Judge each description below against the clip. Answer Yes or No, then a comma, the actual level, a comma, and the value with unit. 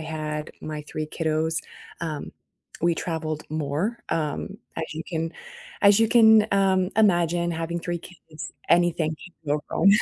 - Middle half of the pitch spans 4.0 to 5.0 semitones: No, average, 2.7 semitones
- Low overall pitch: No, medium, 165 Hz